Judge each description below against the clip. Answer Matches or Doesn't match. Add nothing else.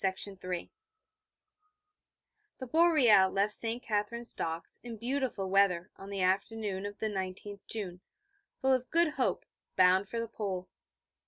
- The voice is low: Doesn't match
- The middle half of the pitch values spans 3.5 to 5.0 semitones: Matches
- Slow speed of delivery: Matches